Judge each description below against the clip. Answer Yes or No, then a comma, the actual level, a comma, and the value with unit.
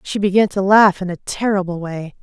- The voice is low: No, high, 190 Hz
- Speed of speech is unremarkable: No, fast, 215 wpm